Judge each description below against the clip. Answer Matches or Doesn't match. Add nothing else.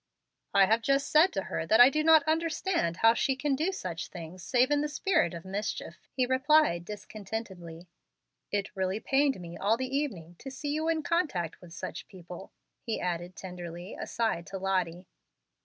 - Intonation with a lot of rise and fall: Matches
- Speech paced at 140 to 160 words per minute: Doesn't match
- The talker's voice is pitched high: Matches